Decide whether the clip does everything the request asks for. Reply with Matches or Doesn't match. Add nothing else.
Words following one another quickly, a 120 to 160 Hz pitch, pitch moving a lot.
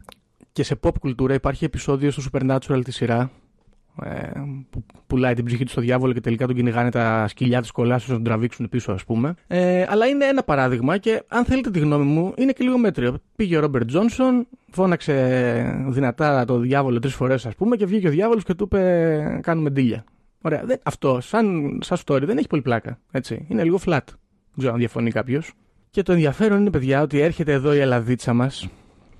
Matches